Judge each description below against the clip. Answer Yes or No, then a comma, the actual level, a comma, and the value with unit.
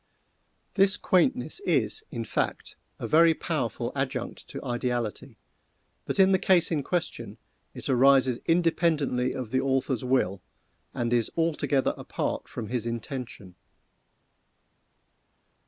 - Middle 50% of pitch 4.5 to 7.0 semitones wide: Yes, wide, 5.4 semitones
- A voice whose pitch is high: No, low, 135 Hz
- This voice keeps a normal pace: No, slow, 120 wpm